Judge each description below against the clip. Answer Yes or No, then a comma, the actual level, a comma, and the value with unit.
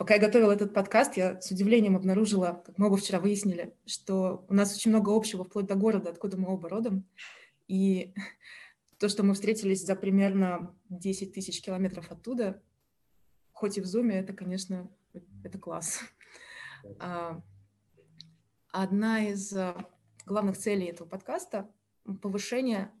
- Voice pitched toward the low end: No, high, 195 Hz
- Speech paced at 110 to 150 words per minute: Yes, average, 140 wpm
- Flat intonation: Yes, narrow, 2.1 semitones